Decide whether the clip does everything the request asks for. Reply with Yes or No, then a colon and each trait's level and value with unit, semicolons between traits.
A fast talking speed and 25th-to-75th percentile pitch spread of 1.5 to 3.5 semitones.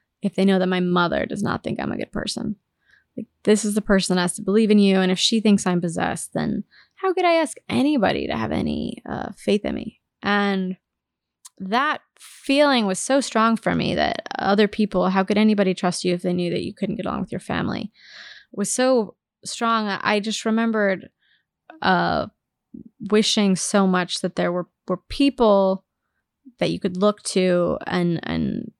No: average, 190 wpm; average, 3.2 semitones